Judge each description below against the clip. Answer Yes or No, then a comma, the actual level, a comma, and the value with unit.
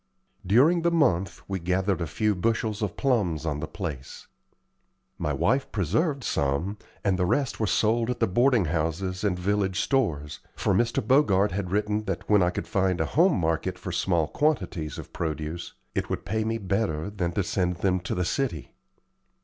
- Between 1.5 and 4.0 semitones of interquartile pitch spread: No, average, 4.6 semitones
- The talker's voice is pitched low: Yes, very low, 95 Hz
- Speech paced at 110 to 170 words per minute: No, average, 180 wpm